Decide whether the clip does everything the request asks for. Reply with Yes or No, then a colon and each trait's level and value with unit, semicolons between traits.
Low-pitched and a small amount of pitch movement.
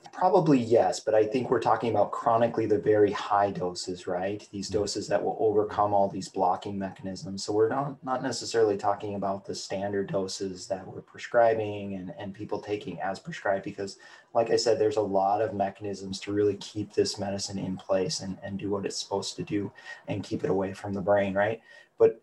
Yes: low, 100 Hz; narrow, 1.8 semitones